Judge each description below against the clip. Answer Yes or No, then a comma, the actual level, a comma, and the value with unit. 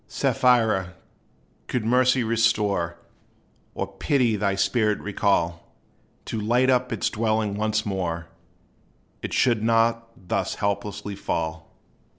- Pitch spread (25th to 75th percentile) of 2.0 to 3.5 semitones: Yes, average, 2.9 semitones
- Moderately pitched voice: No, low, 105 Hz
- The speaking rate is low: Yes, slow, 110 wpm